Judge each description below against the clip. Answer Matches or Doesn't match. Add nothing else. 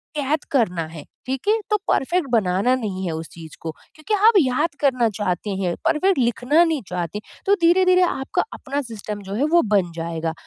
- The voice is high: Matches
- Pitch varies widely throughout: Matches